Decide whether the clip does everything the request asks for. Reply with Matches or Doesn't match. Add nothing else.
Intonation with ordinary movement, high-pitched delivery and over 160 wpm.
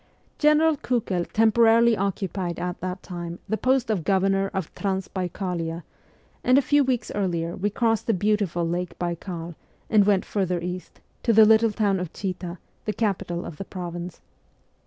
Doesn't match